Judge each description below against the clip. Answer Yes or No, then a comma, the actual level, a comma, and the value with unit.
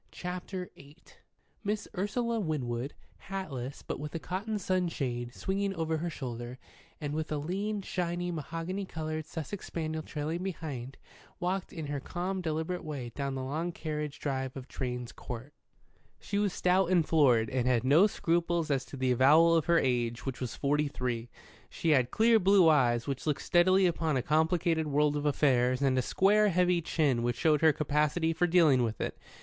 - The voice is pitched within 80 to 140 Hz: No, medium, 155 Hz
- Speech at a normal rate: Yes, average, 175 wpm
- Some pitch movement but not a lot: Yes, average, 4.8 semitones